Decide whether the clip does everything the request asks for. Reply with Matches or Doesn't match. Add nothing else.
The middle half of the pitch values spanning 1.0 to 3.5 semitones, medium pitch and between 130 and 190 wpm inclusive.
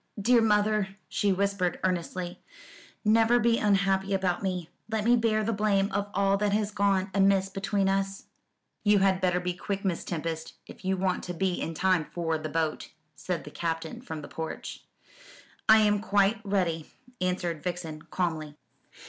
Doesn't match